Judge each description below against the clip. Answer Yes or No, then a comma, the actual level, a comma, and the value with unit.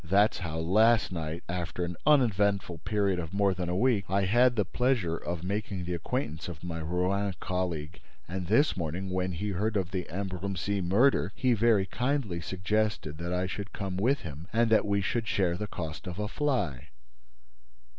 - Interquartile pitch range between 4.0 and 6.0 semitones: No, average, 3.4 semitones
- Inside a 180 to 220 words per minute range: Yes, average, 185 wpm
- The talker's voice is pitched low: Yes, very low, 95 Hz